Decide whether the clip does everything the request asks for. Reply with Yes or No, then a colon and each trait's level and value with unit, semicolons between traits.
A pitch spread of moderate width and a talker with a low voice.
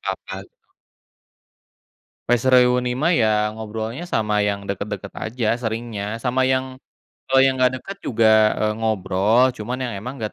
Yes: average, 3.0 semitones; low, 115 Hz